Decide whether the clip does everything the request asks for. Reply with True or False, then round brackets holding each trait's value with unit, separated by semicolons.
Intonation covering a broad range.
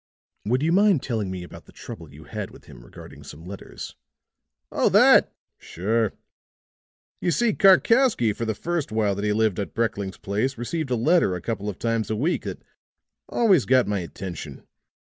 True (7.0 semitones)